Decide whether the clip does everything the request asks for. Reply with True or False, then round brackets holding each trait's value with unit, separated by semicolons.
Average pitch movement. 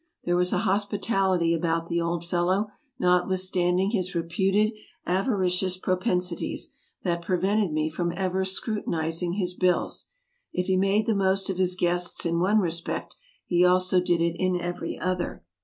False (1.7 semitones)